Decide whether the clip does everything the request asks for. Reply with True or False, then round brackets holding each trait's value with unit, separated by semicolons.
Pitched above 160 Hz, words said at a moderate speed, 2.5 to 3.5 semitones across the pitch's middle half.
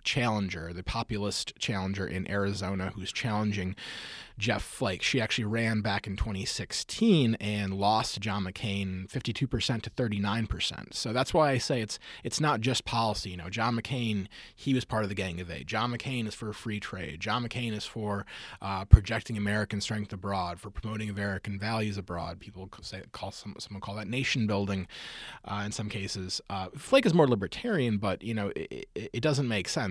False (105 Hz; 185 wpm; 2.9 semitones)